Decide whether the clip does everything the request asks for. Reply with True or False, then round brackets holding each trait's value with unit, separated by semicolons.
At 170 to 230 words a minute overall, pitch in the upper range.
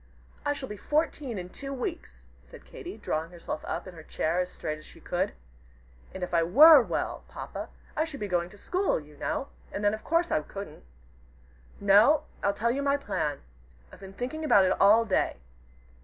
True (200 wpm; 205 Hz)